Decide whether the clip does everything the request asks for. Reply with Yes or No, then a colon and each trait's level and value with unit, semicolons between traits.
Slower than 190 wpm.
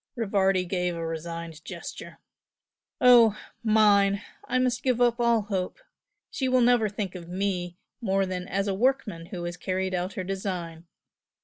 Yes: average, 155 wpm